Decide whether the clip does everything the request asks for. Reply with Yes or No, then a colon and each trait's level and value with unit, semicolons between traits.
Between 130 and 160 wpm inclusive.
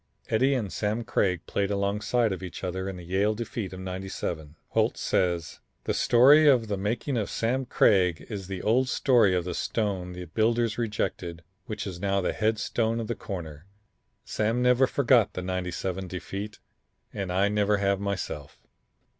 No: average, 170 wpm